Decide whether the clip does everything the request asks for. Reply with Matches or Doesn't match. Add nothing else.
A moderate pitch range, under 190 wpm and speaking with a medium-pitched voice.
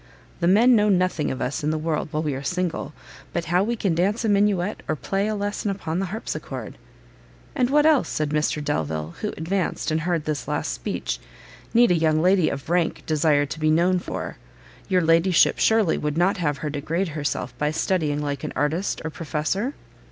Doesn't match